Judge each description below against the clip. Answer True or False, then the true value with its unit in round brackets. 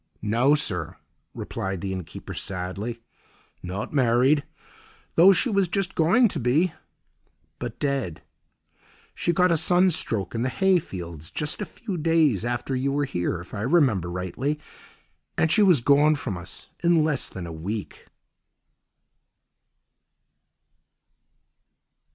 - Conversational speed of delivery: False (125 wpm)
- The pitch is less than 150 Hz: True (135 Hz)